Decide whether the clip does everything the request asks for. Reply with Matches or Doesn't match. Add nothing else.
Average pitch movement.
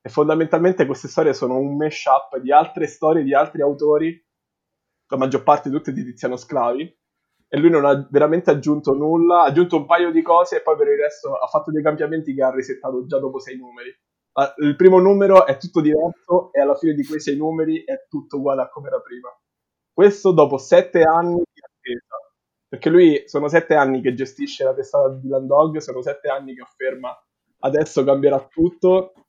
Matches